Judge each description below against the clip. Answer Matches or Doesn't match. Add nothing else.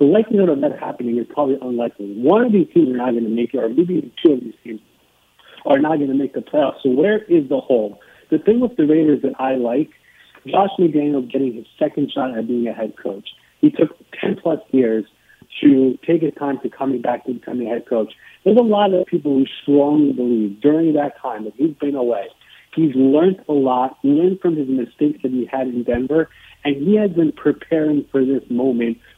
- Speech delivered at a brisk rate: Matches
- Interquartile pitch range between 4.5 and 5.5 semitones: Matches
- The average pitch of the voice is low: Doesn't match